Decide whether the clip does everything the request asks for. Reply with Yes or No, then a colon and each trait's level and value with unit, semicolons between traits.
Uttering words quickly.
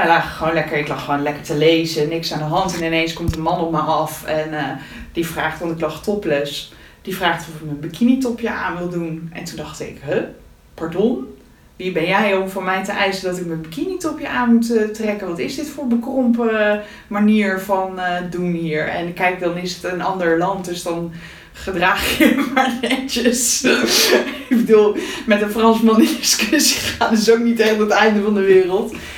Yes: fast, 215 wpm